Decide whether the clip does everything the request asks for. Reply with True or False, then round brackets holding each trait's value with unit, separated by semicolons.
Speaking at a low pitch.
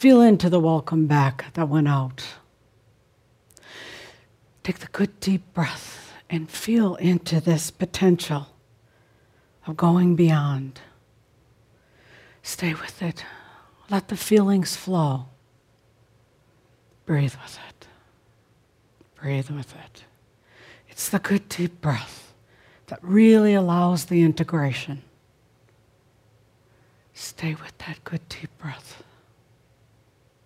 False (145 Hz)